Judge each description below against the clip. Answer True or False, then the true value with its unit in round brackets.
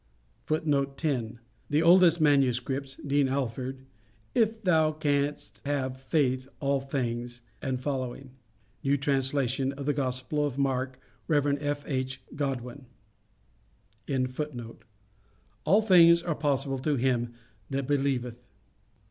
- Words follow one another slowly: True (105 wpm)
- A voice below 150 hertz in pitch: True (140 Hz)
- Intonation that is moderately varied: False (2.1 semitones)